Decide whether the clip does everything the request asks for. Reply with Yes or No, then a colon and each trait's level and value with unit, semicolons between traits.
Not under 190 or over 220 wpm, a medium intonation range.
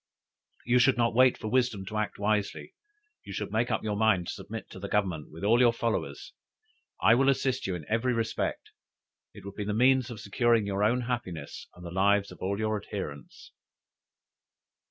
Yes: average, 195 wpm; average, 3.3 semitones